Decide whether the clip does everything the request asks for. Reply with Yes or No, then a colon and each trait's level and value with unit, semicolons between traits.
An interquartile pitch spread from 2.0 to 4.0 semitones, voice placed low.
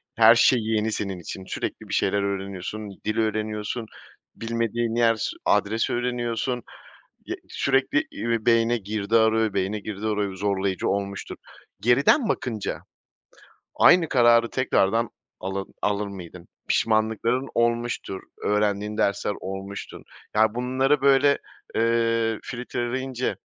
Yes: average, 2.8 semitones; low, 110 Hz